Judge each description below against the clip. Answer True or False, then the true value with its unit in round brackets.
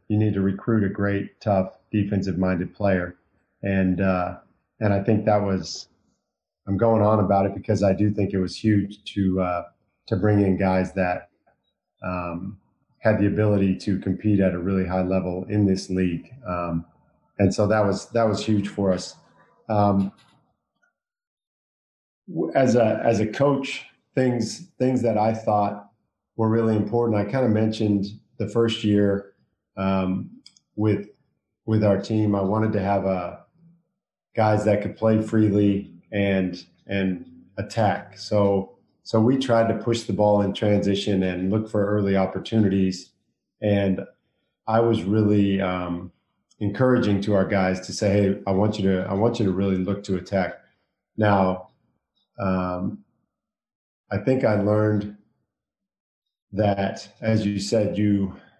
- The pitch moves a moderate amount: False (2.2 semitones)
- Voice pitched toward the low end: True (100 Hz)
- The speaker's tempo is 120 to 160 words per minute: True (155 wpm)